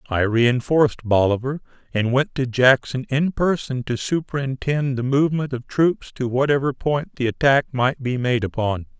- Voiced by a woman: No, male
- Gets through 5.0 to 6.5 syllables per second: No, 4.7 syllables/s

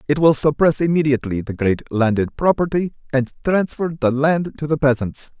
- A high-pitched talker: No, medium, 140 Hz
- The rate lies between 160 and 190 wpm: Yes, average, 165 wpm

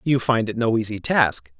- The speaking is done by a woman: No, male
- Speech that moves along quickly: Yes, fast, 225 wpm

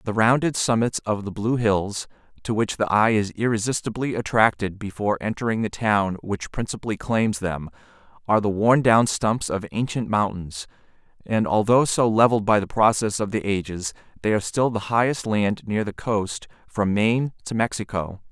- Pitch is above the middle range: No, low, 105 Hz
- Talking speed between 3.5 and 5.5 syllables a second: Yes, 5.1 syllables/s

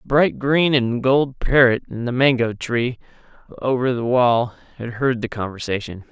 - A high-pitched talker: No, low, 125 Hz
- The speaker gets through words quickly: No, average, 165 wpm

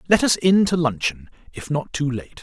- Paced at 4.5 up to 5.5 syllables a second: Yes, 5.0 syllables/s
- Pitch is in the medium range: Yes, medium, 150 Hz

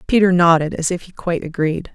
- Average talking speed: No, fast, 215 wpm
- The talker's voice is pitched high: No, medium, 170 Hz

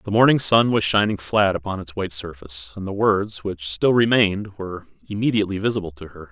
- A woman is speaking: No, male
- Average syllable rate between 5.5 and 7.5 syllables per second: Yes, 6.0 syllables/s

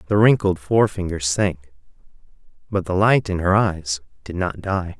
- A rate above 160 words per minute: No, average, 155 wpm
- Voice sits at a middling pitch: No, very low, 95 Hz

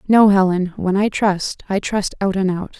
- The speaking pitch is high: Yes, high, 195 Hz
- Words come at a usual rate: No, fast, 215 wpm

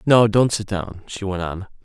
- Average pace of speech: No, fast, 230 wpm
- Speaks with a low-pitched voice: Yes, low, 100 Hz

